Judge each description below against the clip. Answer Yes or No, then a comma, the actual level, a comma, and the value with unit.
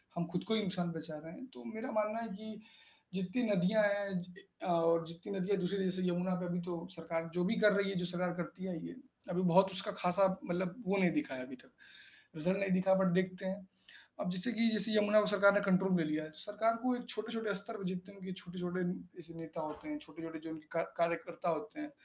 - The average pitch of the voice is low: No, medium, 185 Hz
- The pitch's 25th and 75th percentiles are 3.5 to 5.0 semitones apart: No, average, 2.9 semitones